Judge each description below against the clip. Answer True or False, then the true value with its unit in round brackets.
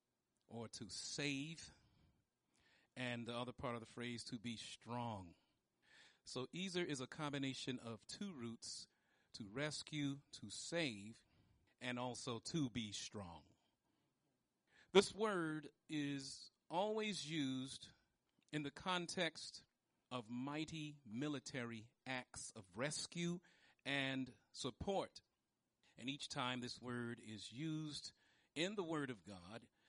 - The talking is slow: True (115 wpm)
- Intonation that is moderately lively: True (4.4 semitones)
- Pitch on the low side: True (130 Hz)